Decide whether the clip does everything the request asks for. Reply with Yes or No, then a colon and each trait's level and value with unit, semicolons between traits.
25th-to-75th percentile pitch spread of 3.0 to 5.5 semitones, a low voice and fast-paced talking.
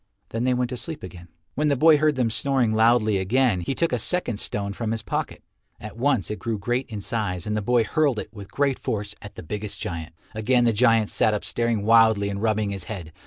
Yes: average, 3.4 semitones; low, 110 Hz; fast, 235 wpm